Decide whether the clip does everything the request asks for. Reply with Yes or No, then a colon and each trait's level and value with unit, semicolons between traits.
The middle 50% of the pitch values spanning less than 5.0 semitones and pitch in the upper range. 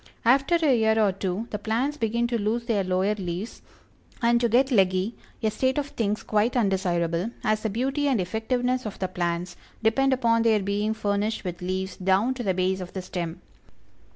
Yes: average, 4.1 semitones; high, 215 Hz